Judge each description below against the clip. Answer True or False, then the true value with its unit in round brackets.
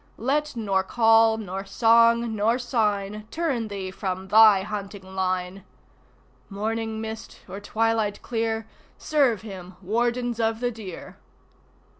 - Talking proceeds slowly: True (120 wpm)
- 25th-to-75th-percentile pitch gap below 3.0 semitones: True (2.6 semitones)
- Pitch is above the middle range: True (220 Hz)